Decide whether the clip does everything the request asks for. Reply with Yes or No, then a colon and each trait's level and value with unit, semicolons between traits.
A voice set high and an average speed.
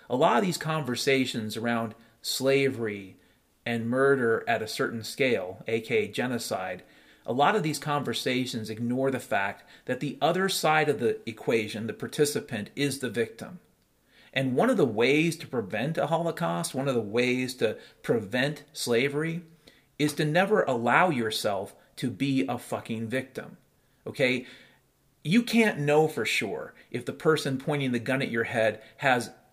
No: low, 135 Hz; average, 155 wpm